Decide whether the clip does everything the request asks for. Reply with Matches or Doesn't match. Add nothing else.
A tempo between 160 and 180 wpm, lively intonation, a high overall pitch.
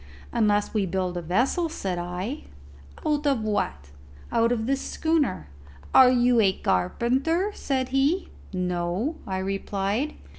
Doesn't match